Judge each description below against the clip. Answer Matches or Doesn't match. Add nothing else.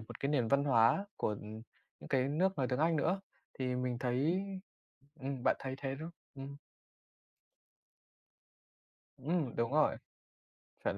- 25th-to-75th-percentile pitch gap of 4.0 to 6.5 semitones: Doesn't match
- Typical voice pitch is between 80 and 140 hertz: Matches